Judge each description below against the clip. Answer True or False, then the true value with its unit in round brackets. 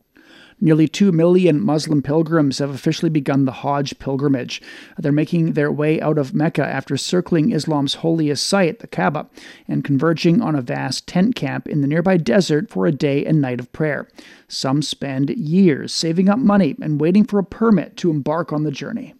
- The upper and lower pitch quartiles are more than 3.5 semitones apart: True (4.1 semitones)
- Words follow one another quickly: False (185 wpm)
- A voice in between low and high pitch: True (155 Hz)